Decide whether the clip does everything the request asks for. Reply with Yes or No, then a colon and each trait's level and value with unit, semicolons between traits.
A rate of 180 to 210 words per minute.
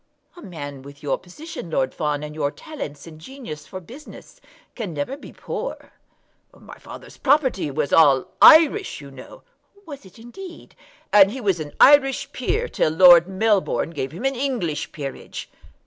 No: average, 165 wpm